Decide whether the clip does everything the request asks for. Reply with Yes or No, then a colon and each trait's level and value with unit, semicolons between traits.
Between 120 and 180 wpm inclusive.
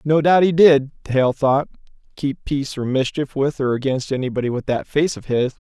No: average, 200 wpm